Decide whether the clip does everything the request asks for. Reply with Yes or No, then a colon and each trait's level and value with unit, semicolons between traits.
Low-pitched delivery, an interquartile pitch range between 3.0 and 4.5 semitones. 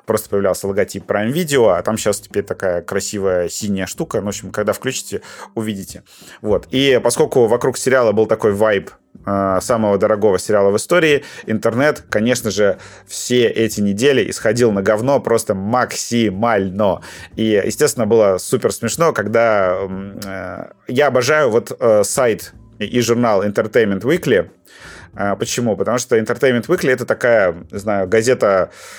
Yes: low, 110 Hz; average, 3.4 semitones